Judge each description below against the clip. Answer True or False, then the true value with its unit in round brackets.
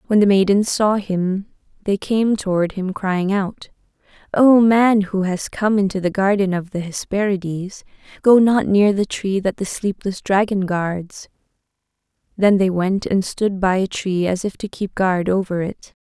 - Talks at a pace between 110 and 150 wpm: False (175 wpm)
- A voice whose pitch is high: True (195 Hz)